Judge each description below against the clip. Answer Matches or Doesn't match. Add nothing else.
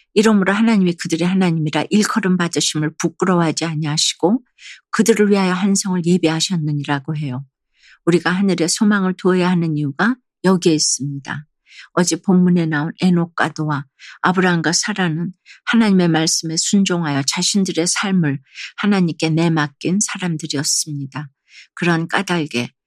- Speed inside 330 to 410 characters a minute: Matches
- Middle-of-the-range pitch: Matches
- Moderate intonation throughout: Matches